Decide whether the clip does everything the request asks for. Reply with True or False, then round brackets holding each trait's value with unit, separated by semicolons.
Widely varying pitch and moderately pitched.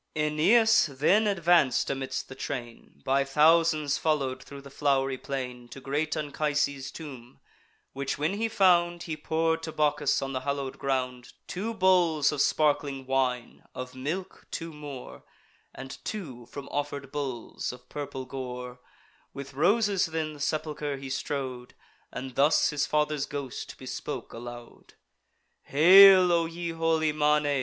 False (3.4 semitones; 145 Hz)